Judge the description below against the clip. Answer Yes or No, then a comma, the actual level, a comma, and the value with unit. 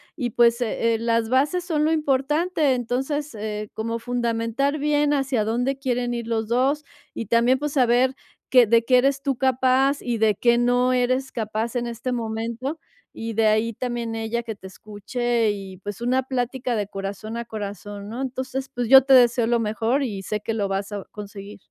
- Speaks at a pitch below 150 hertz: No, high, 240 Hz